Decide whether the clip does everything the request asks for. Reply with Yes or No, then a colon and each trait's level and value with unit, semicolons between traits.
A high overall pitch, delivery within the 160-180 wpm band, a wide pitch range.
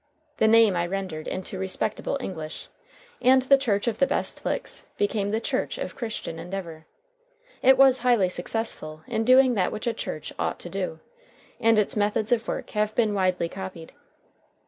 No: high, 210 Hz; average, 170 wpm; average, 4.3 semitones